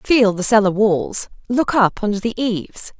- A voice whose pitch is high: Yes, high, 215 Hz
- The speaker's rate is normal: Yes, average, 180 wpm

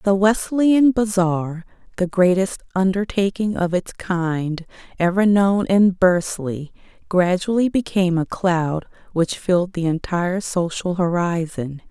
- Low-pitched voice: No, medium, 185 Hz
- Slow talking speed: Yes, slow, 115 wpm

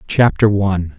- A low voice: Yes, low, 100 Hz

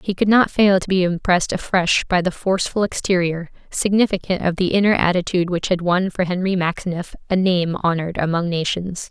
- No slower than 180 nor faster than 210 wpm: Yes, average, 185 wpm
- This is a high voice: No, medium, 180 Hz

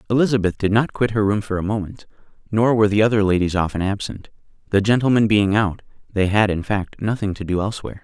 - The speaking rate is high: Yes, fast, 210 wpm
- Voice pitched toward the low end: Yes, low, 105 Hz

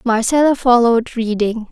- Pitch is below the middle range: No, high, 235 Hz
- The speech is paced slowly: Yes, slow, 105 wpm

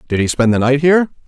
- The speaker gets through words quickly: Yes, fast, 280 wpm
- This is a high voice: No, low, 135 Hz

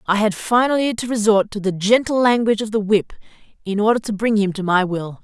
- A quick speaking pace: Yes, fast, 230 wpm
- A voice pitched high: Yes, high, 210 Hz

